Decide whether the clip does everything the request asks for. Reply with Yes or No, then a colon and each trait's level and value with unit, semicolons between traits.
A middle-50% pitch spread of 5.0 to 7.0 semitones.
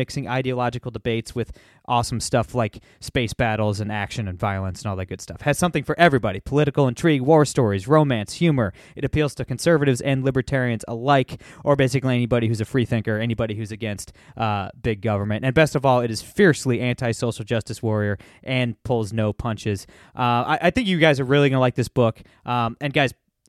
No: average, 3.8 semitones